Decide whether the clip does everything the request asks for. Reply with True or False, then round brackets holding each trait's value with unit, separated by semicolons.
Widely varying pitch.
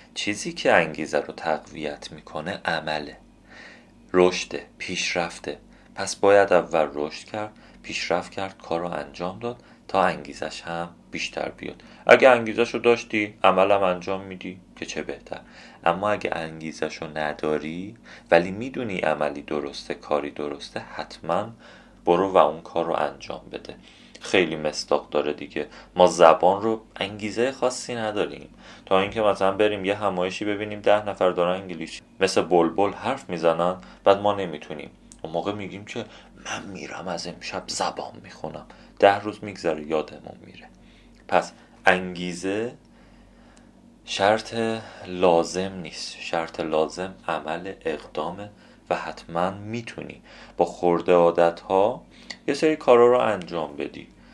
False (3.8 semitones)